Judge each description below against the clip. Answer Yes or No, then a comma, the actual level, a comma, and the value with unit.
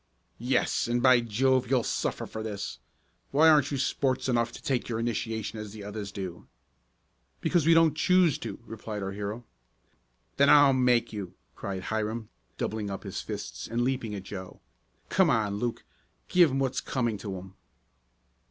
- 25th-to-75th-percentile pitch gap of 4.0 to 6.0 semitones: Yes, average, 4.3 semitones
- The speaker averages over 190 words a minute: No, average, 170 wpm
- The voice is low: Yes, low, 115 Hz